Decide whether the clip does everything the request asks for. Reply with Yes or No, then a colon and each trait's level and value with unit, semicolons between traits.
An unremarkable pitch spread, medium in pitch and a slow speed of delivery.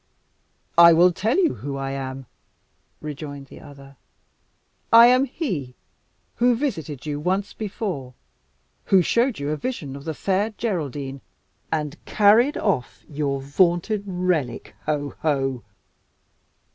No: wide, 6.8 semitones; medium, 155 Hz; slow, 125 wpm